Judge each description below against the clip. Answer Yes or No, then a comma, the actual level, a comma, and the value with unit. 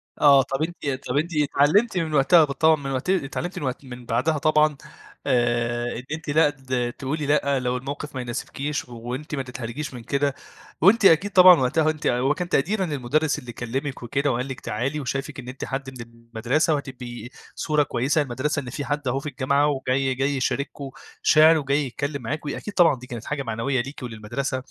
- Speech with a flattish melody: No, average, 3.2 semitones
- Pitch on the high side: No, medium, 140 Hz